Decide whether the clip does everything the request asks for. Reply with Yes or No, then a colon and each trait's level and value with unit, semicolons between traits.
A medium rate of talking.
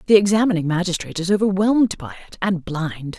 Yes: average, 150 wpm